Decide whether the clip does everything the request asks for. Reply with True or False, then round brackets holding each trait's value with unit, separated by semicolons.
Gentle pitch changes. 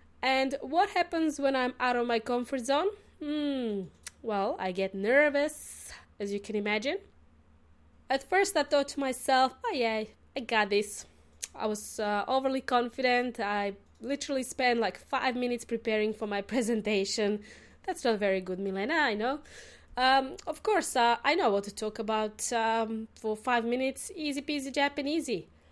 False (4.5 semitones)